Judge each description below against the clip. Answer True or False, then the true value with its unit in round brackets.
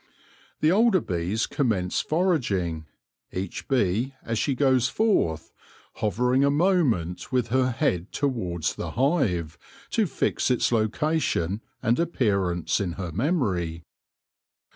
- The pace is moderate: False (120 wpm)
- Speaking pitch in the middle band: False (115 Hz)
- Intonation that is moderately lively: False (8.0 semitones)